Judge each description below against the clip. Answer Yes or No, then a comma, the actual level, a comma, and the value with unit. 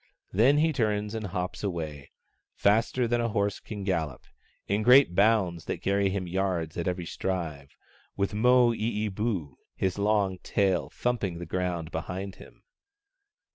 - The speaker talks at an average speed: Yes, average, 150 wpm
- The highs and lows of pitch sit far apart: No, average, 3.7 semitones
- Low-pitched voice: Yes, low, 100 Hz